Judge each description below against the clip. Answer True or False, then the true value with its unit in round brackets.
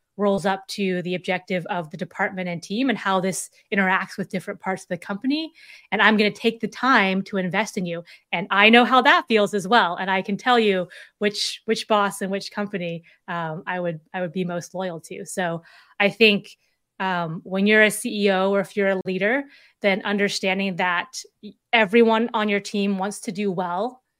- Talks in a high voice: True (200 Hz)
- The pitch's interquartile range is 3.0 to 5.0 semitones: False (2.5 semitones)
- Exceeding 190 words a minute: True (205 wpm)